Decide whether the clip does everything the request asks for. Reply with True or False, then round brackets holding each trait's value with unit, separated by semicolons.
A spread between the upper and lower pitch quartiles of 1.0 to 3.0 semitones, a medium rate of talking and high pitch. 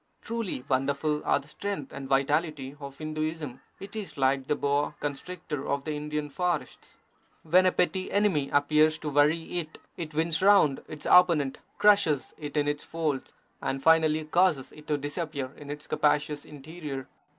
False (2.6 semitones; 160 wpm; 150 Hz)